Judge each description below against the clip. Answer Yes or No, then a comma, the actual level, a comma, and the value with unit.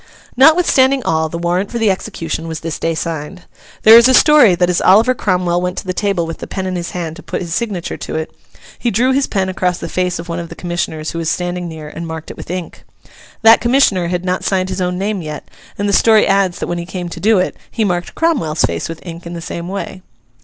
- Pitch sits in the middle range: Yes, medium, 180 Hz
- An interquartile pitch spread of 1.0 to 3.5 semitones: Yes, average, 3.2 semitones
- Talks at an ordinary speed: No, fast, 255 wpm